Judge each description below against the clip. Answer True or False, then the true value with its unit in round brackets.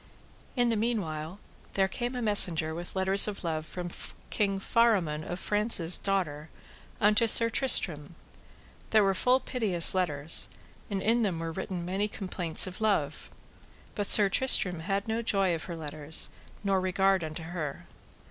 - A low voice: False (190 Hz)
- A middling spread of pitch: True (4.2 semitones)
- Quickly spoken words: False (155 wpm)